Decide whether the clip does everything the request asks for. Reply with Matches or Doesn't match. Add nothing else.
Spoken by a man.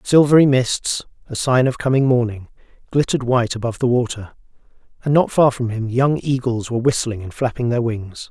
Matches